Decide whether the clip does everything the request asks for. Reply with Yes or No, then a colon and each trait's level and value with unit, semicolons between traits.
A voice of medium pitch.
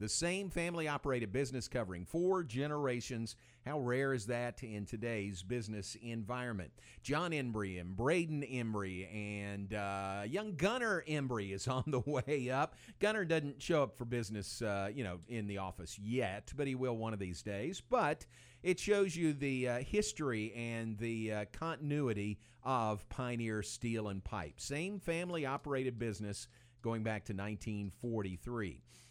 No: low, 120 Hz